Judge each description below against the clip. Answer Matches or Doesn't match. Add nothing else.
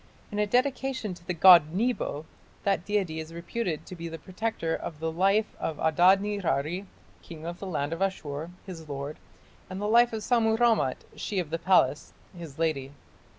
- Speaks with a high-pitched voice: Doesn't match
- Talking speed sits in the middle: Matches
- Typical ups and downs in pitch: Matches